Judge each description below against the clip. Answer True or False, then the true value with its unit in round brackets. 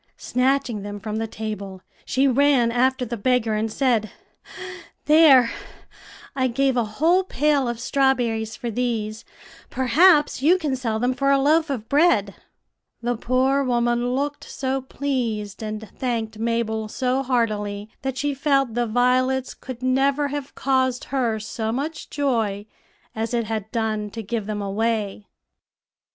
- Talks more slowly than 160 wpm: True (145 wpm)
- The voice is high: True (245 Hz)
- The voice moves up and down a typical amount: True (3.5 semitones)